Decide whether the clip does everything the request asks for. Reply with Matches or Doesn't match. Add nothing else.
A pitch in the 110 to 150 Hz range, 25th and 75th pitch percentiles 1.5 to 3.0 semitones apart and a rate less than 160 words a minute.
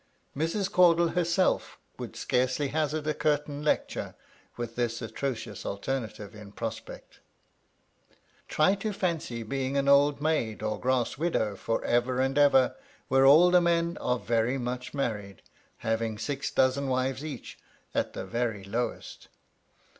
Doesn't match